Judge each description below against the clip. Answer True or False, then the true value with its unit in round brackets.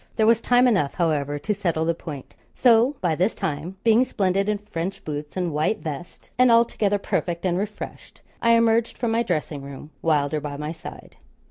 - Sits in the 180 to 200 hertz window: True (185 Hz)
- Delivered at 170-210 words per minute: True (190 wpm)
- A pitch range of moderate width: False (6.6 semitones)